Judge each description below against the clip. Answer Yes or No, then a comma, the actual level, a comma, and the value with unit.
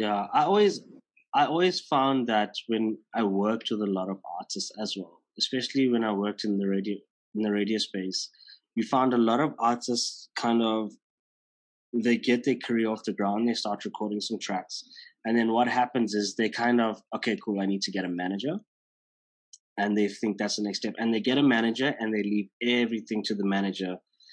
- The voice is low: Yes, low, 110 Hz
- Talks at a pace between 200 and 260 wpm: Yes, fast, 205 wpm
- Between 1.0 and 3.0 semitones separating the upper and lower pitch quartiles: Yes, average, 2.7 semitones